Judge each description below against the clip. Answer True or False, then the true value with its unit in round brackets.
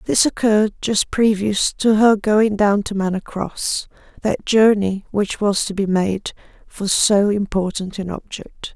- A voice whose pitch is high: True (205 Hz)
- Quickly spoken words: False (150 wpm)